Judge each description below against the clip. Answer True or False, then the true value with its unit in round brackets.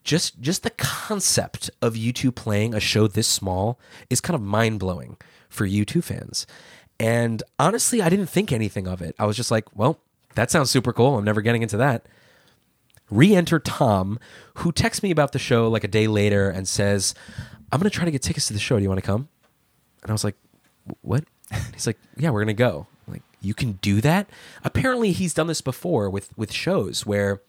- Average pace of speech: False (210 wpm)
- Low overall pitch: True (115 Hz)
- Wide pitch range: True (6.1 semitones)